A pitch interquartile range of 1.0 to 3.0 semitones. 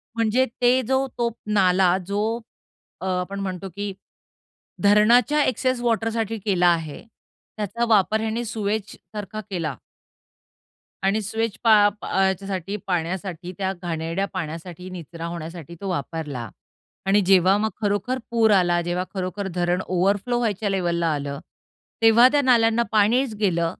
No: average, 3.9 semitones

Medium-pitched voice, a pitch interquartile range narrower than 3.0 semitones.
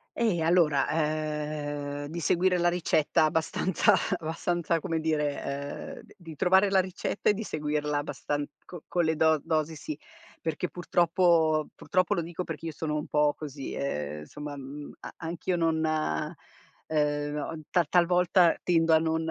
Yes: medium, 160 Hz; narrow, 2.6 semitones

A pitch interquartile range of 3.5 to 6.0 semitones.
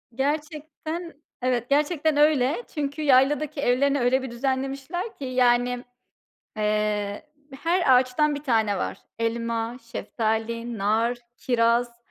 Yes: average, 4.0 semitones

